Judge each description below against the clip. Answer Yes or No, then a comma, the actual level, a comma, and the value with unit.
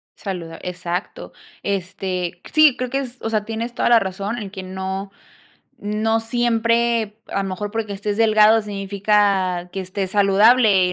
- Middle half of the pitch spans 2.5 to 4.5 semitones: Yes, average, 3.0 semitones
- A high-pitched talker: Yes, high, 205 Hz